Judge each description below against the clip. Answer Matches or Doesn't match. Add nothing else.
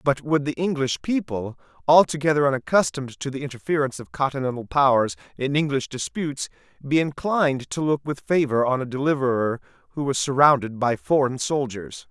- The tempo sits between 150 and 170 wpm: Matches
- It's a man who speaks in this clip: Matches